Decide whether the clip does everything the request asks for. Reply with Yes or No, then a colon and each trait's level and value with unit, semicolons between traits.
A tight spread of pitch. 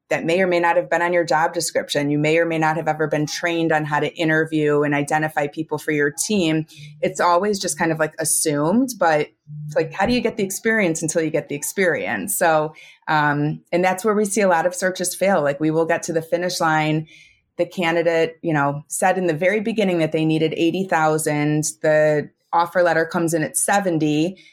Yes: narrow, 2.3 semitones